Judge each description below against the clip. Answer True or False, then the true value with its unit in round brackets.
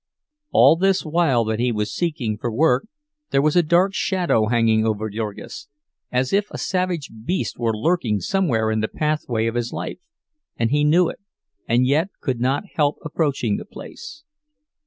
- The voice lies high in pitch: False (135 Hz)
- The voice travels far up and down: True (7.1 semitones)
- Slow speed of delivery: False (175 wpm)